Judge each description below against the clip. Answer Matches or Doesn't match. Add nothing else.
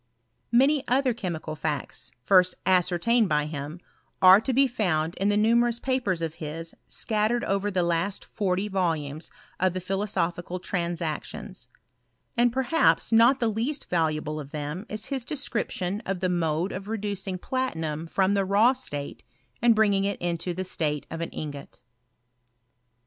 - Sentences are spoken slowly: Doesn't match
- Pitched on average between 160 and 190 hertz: Matches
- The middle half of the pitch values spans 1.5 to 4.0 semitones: Doesn't match